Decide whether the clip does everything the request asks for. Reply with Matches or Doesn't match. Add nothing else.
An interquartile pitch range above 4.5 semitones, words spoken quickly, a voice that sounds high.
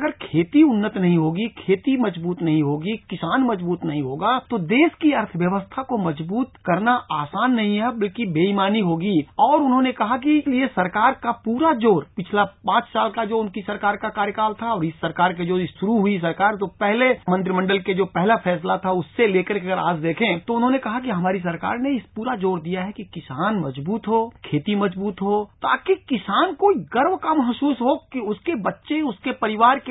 Matches